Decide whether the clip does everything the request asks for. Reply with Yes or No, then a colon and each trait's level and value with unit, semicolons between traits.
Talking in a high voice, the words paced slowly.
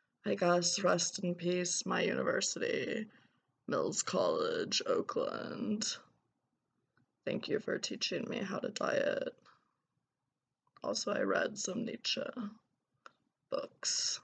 Yes: high, 240 Hz; slow, 100 wpm